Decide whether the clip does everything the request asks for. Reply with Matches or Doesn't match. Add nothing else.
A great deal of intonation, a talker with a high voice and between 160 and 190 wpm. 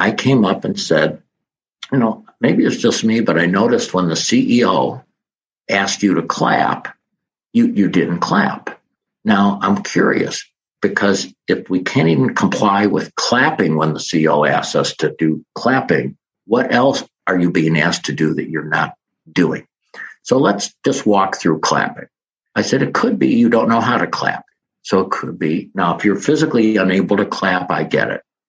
Doesn't match